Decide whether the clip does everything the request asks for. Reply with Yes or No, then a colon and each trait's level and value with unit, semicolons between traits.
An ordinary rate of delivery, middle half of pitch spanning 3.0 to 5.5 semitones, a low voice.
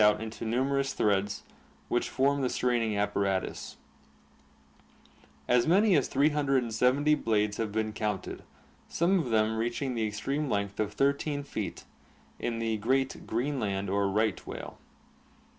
Yes: average, 145 wpm; average, 4.6 semitones; low, 115 Hz